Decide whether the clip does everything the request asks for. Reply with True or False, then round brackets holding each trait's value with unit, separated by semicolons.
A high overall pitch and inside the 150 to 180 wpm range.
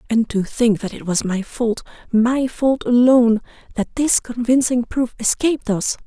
True (235 Hz; 170 wpm)